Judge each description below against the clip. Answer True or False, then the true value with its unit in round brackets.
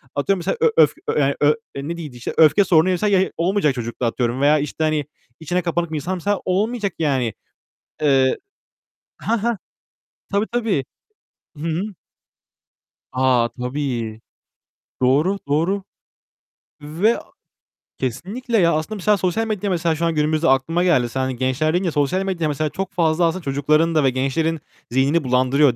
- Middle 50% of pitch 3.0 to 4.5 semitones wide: False (5.2 semitones)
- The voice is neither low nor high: True (155 Hz)